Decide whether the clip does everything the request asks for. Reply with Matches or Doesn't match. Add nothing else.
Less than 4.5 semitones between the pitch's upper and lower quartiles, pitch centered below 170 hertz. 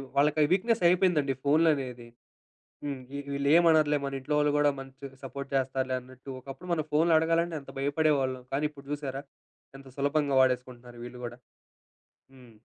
Matches